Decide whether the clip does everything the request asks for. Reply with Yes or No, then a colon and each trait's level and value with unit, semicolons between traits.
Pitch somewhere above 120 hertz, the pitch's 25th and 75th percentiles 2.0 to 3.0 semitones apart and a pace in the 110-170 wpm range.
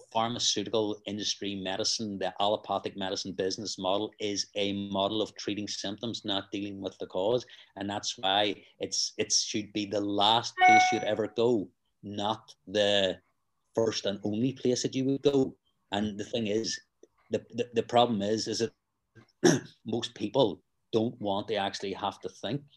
No: low, 105 Hz; average, 2.7 semitones; average, 165 wpm